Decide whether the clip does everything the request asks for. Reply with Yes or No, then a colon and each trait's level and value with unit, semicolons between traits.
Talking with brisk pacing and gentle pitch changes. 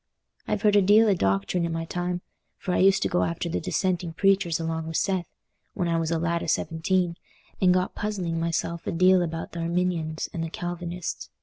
Yes: fast, 210 wpm; narrow, 1.9 semitones